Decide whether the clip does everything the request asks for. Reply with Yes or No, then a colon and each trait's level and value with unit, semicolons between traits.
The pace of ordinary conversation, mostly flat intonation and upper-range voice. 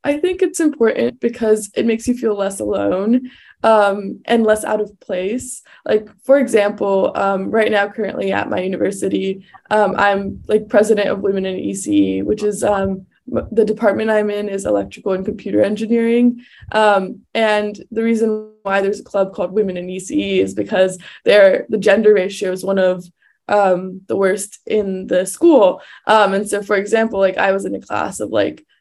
Yes: average, 180 wpm; narrow, 2.3 semitones; high, 205 Hz